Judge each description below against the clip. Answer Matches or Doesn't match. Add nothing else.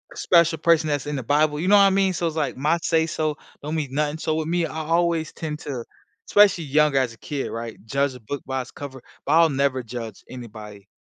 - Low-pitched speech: Doesn't match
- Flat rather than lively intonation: Doesn't match